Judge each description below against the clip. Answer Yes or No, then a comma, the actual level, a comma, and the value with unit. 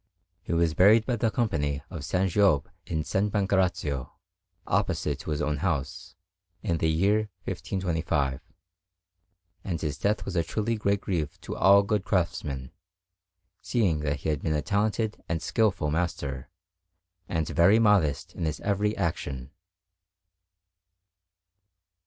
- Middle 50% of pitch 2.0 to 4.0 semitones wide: No, average, 5.1 semitones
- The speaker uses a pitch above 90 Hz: No, very low, 85 Hz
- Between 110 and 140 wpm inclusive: Yes, slow, 135 wpm